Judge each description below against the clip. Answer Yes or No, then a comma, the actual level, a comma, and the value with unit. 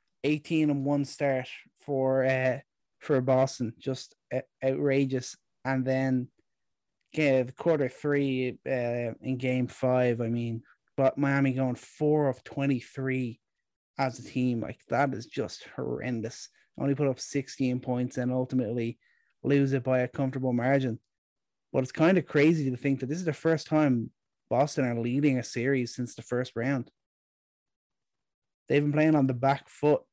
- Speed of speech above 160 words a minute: No, average, 155 wpm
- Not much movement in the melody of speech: Yes, narrow, 2.0 semitones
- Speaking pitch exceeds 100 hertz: Yes, low, 130 Hz